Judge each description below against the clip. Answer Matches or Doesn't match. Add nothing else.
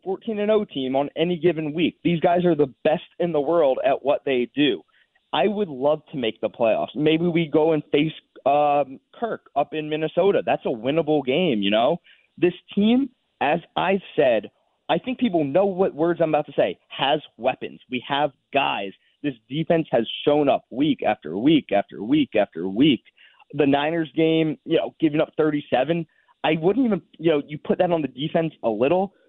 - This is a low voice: Doesn't match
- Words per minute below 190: Doesn't match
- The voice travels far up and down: Doesn't match